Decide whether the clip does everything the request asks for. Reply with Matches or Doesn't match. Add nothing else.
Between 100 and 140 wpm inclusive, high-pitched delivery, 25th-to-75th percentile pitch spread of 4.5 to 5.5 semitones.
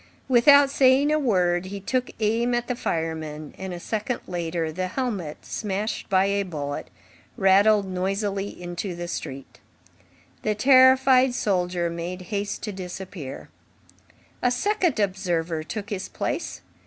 Matches